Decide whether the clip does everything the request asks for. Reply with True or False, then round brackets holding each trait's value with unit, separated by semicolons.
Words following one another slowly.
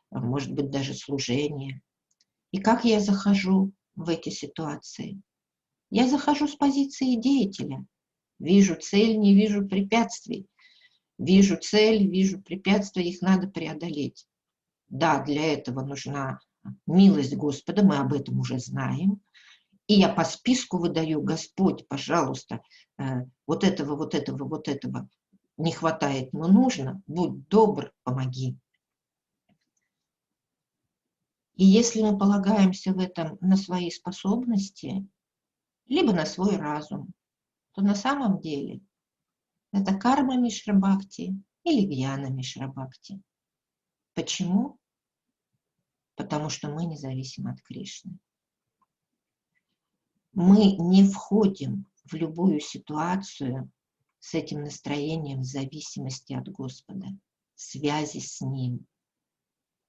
True (105 wpm)